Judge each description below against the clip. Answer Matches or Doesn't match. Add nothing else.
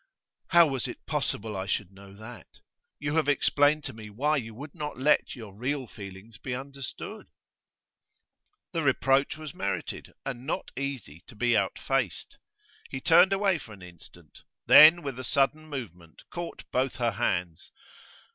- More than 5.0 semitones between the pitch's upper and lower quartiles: Matches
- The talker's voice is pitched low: Matches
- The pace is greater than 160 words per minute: Doesn't match